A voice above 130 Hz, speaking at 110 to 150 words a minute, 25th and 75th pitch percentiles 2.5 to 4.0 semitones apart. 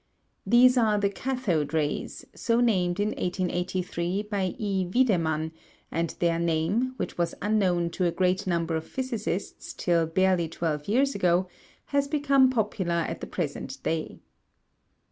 No: medium, 185 Hz; average, 145 wpm; average, 4.6 semitones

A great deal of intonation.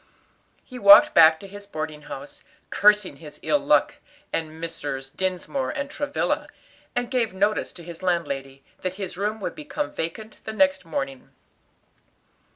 Yes: wide, 7.3 semitones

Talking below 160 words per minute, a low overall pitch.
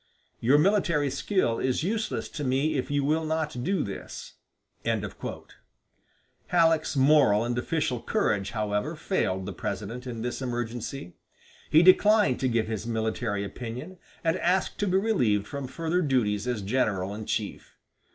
Yes: average, 145 wpm; low, 130 Hz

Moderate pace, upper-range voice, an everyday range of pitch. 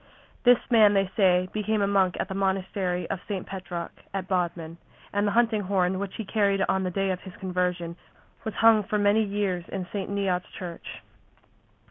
No: average, 185 wpm; high, 195 Hz; narrow, 2.0 semitones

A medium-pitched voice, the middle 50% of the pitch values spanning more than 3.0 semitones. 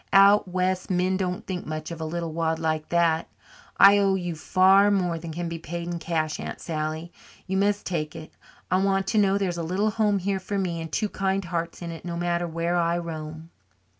No: medium, 175 Hz; average, 2.7 semitones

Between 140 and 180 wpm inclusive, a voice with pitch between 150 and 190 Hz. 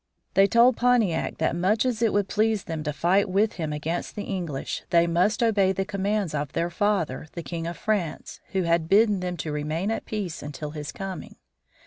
No: average, 200 wpm; medium, 185 Hz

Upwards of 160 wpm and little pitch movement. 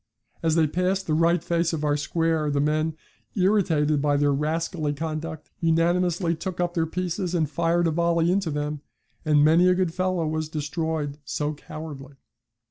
Yes: average, 170 wpm; narrow, 2.3 semitones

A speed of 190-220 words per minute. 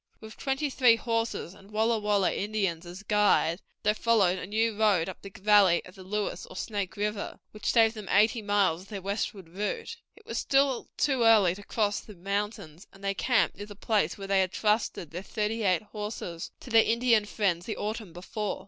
Yes: average, 200 wpm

